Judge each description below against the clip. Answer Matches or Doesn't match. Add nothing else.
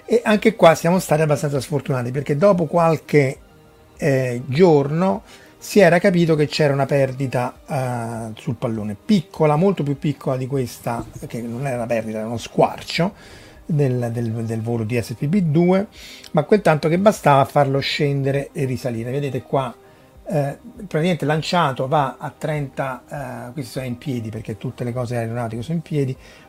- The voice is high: Doesn't match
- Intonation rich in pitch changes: Doesn't match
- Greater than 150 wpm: Matches